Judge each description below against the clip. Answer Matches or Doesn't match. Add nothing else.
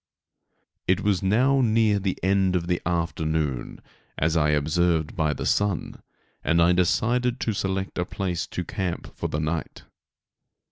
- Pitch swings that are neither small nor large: Matches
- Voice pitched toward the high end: Doesn't match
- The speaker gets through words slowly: Doesn't match